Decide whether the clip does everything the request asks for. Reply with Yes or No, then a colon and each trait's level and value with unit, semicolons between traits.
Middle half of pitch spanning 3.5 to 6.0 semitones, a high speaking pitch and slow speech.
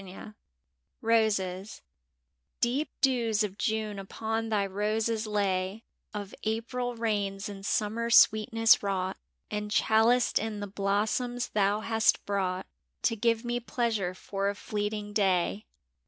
No: narrow, 2.4 semitones; high, 210 Hz; slow, 120 wpm